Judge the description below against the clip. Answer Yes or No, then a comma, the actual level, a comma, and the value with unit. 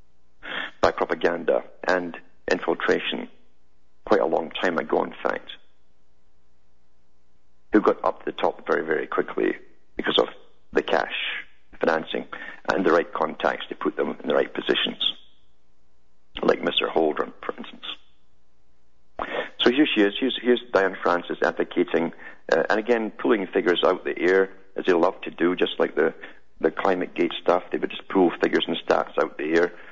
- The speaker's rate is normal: Yes, average, 160 wpm